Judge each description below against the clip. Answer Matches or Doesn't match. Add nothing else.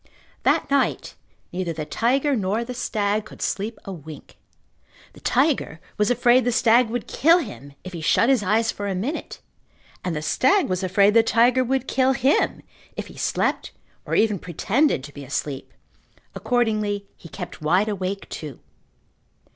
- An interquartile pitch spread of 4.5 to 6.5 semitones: Matches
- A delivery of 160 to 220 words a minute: Matches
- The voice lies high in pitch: Matches